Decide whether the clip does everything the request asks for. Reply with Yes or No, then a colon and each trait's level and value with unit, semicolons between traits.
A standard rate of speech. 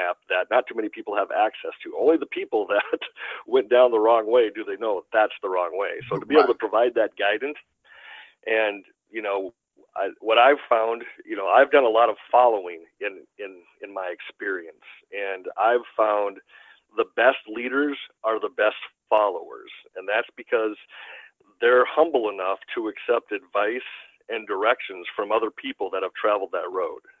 Yes: average, 175 wpm